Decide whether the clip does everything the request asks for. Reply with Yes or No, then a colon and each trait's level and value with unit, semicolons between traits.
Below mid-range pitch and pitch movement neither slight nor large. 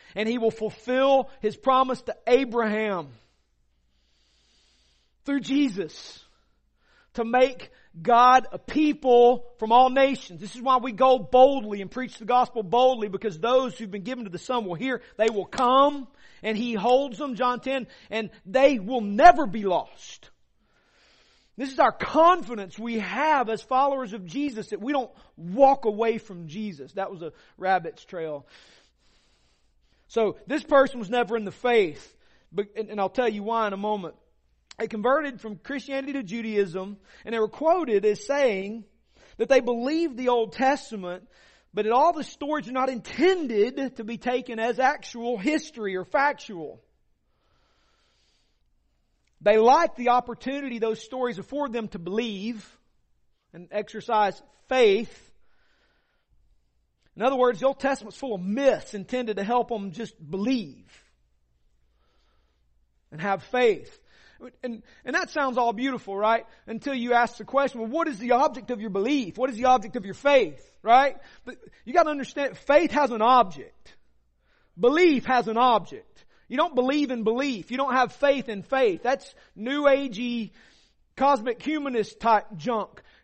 No: high, 240 Hz; average, 4.4 semitones